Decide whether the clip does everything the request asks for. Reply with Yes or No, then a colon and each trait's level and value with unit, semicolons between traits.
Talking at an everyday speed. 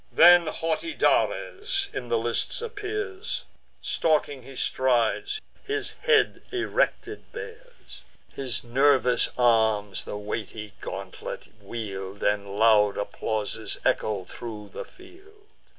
No: slow, 105 wpm